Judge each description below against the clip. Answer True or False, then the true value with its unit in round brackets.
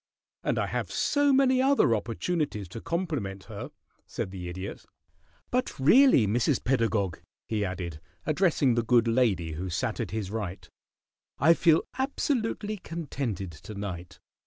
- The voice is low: True (115 Hz)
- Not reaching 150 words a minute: True (140 wpm)